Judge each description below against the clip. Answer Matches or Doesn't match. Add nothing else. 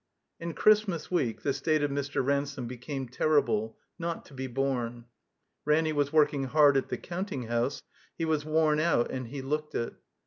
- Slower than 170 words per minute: Doesn't match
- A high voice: Doesn't match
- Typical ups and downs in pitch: Matches